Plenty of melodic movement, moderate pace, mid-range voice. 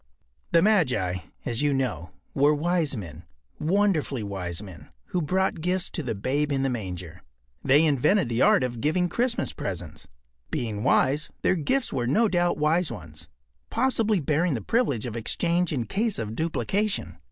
Yes: wide, 8.0 semitones; average, 160 wpm; medium, 145 Hz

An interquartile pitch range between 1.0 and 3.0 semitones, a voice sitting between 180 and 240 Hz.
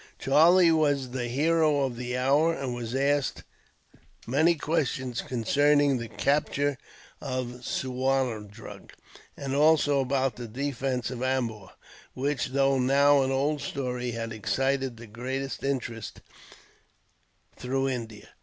No: narrow, 2.4 semitones; low, 135 Hz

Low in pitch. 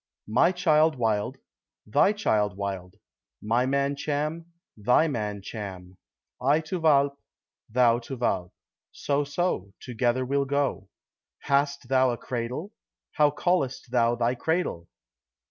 Yes: low, 130 Hz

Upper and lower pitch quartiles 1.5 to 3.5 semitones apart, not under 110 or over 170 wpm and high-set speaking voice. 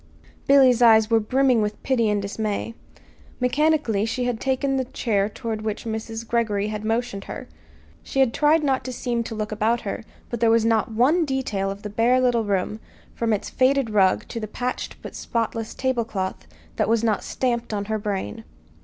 No: average, 2.9 semitones; average, 190 wpm; high, 230 Hz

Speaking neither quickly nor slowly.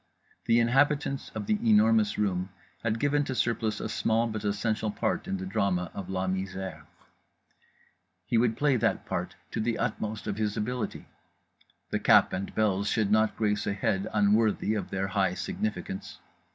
Yes: average, 165 wpm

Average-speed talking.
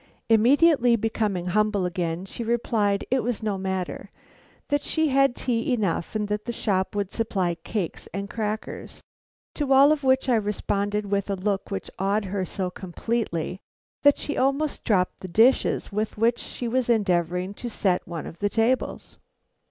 Yes: average, 165 wpm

